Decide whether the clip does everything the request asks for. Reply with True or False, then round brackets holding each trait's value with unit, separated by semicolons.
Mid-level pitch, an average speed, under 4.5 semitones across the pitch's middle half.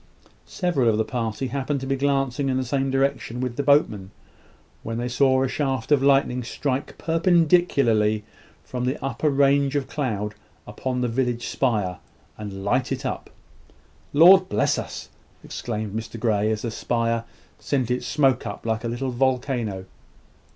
False (130 Hz; 160 wpm; 3.3 semitones)